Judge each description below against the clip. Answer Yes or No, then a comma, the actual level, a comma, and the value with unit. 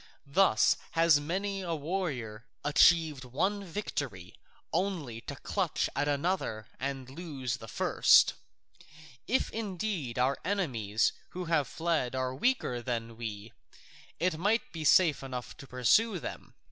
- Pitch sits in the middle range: Yes, medium, 145 Hz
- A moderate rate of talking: No, slow, 130 wpm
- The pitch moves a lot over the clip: Yes, wide, 6.5 semitones